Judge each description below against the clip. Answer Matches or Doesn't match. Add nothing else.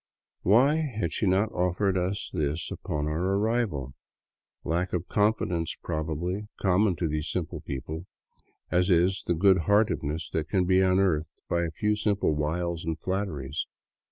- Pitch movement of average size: Matches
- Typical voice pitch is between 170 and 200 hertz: Doesn't match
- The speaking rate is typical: Matches